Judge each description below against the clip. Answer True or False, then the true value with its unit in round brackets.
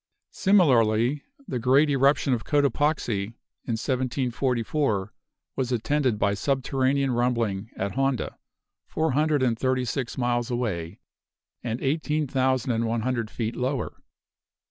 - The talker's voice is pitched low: True (125 Hz)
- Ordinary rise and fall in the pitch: True (3.1 semitones)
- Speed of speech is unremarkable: False (120 wpm)